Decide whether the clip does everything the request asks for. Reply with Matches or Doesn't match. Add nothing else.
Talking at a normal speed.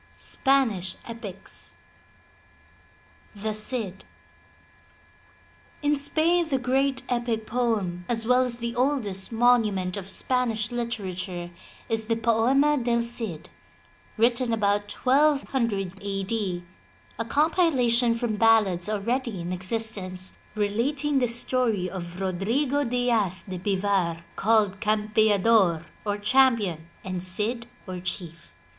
Doesn't match